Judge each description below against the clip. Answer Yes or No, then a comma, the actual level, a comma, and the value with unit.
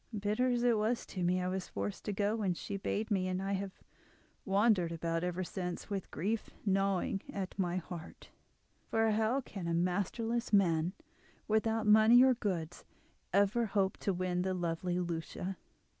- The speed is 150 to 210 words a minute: Yes, average, 170 wpm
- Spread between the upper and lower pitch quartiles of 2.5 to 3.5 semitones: Yes, average, 3.2 semitones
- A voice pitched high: Yes, high, 195 Hz